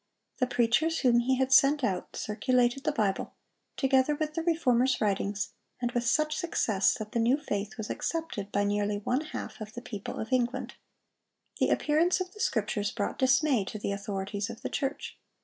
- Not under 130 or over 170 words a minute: No, average, 185 wpm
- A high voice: Yes, high, 240 Hz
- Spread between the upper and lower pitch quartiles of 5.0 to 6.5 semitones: Yes, average, 5.3 semitones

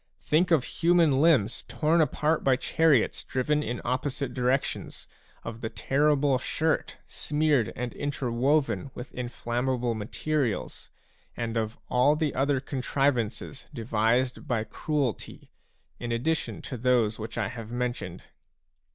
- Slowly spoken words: Yes, slow, 125 wpm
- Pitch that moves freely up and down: No, average, 3.9 semitones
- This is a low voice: Yes, low, 130 Hz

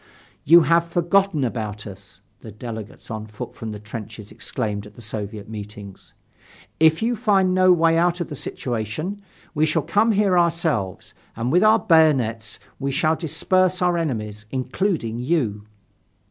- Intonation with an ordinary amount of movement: No, wide, 8.2 semitones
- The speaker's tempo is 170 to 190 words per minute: No, average, 155 wpm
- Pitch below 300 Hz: Yes, medium, 140 Hz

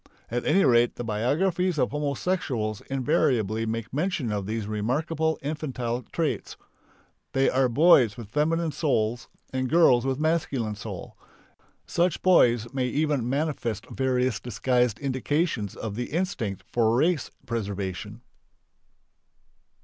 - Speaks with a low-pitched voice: Yes, low, 125 Hz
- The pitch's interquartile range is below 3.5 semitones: No, average, 5.1 semitones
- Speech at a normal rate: No, slow, 125 wpm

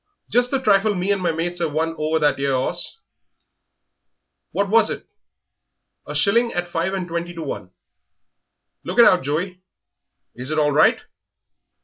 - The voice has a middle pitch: Yes, medium, 175 Hz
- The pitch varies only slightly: No, average, 4.3 semitones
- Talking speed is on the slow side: No, average, 160 wpm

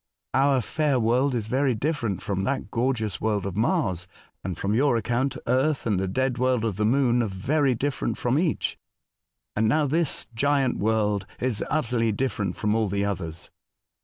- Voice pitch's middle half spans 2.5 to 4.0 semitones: No, average, 4.5 semitones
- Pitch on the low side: Yes, low, 120 Hz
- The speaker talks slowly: No, average, 175 wpm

